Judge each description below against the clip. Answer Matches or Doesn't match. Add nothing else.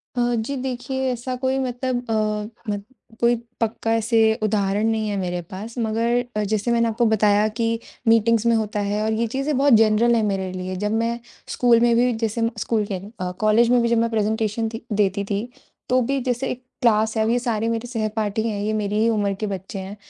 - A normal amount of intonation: Doesn't match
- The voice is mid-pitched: Doesn't match